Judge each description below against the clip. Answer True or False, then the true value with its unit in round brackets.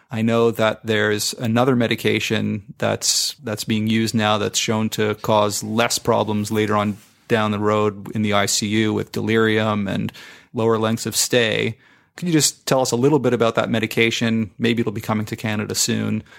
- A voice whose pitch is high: False (110 Hz)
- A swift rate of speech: False (190 wpm)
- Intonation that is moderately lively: False (1.4 semitones)